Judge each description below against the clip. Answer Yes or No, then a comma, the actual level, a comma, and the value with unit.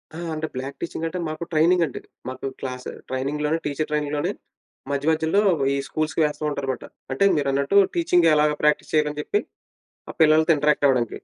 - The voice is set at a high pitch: No, medium, 150 Hz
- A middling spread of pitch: No, narrow, 2.2 semitones